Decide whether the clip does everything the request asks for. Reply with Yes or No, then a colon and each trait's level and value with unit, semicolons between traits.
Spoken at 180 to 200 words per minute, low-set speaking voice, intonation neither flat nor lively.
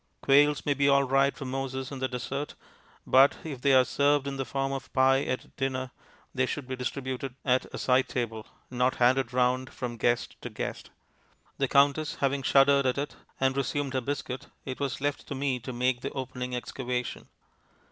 No: average, 190 wpm; low, 130 Hz; narrow, 1.5 semitones